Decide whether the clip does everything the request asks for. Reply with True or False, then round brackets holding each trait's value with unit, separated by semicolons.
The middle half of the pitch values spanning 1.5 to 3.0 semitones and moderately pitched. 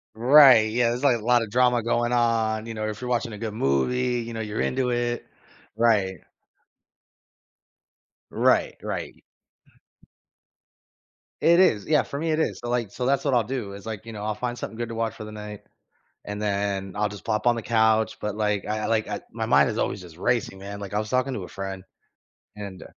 False (2.7 semitones; 110 Hz)